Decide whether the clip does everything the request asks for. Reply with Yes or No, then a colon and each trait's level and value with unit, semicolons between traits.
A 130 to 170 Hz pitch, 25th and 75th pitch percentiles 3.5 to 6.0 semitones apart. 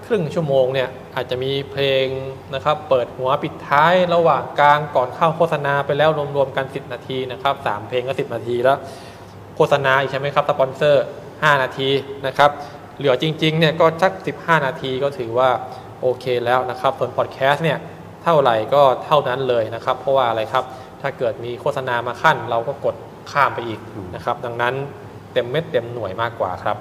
No: low, 135 Hz; narrow, 2.5 semitones